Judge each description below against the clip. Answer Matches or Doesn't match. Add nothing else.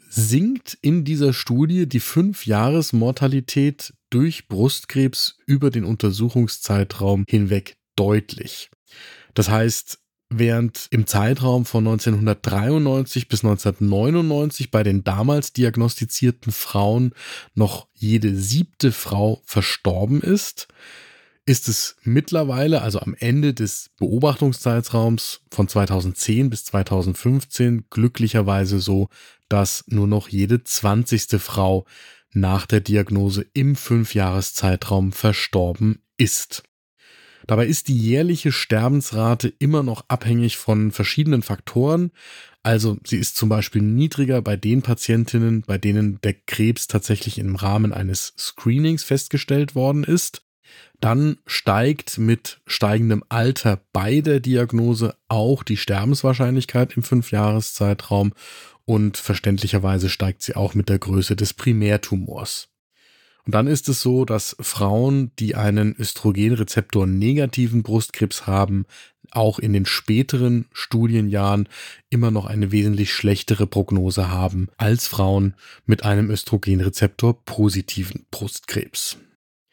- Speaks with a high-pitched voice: Doesn't match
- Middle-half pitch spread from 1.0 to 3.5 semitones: Doesn't match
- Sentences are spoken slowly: Matches